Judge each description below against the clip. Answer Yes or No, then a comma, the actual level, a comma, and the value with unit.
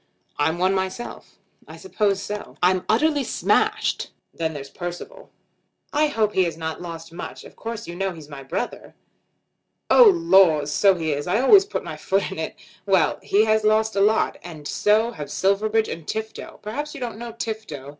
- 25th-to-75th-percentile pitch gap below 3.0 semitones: No, average, 5.0 semitones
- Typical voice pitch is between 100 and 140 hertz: No, high, 195 Hz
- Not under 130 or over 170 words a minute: No, average, 185 wpm